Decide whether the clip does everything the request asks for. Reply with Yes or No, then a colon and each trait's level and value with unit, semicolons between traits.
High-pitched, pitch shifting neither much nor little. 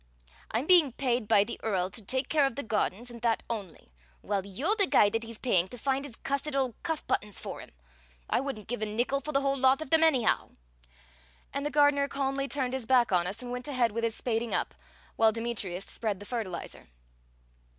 Yes: high, 245 Hz; average, 4.2 semitones